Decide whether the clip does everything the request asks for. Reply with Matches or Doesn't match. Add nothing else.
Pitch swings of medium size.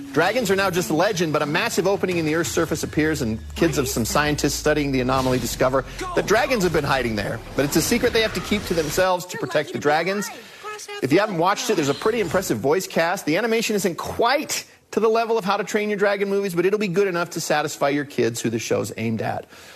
Doesn't match